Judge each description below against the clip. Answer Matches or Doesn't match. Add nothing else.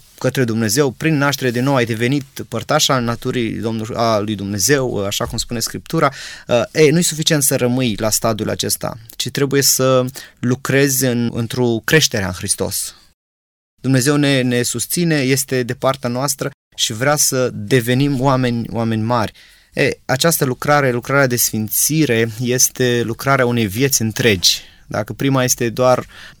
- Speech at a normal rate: Matches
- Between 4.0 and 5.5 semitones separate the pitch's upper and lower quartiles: Doesn't match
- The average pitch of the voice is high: Doesn't match